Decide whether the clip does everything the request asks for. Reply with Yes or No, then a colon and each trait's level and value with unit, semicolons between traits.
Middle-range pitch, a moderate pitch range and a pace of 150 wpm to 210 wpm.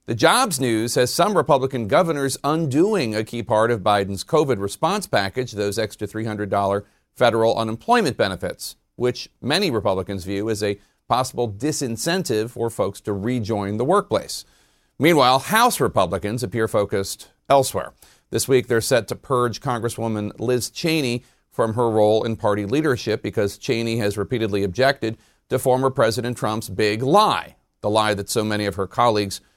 No: low, 115 Hz; average, 3.5 semitones; average, 155 wpm